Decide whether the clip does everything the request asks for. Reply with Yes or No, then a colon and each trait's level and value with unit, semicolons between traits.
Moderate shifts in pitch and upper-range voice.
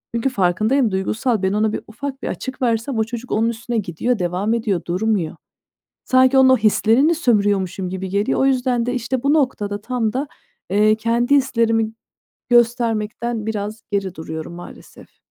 Yes: average, 3.5 semitones; high, 225 Hz